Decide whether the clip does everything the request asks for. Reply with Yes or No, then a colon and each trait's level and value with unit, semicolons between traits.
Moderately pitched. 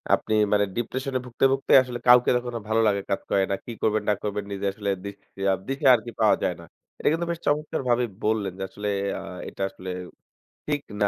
No: low, 110 Hz